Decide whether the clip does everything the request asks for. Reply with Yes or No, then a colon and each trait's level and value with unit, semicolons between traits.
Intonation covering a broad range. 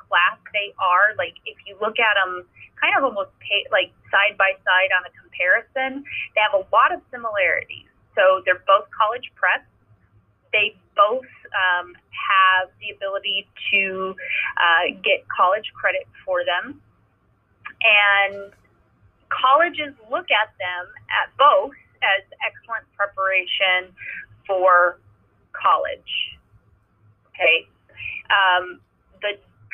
Yes: wide, 6.7 semitones